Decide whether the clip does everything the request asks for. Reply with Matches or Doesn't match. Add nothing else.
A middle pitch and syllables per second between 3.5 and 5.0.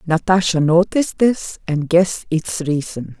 Matches